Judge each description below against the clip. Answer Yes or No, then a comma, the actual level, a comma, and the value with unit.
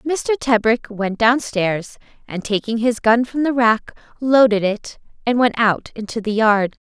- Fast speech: No, average, 165 wpm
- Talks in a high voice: Yes, high, 230 Hz